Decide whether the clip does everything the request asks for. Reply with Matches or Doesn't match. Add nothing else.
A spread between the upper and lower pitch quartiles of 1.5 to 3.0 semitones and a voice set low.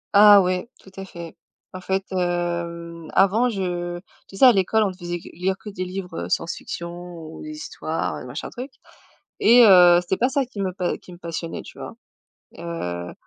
Doesn't match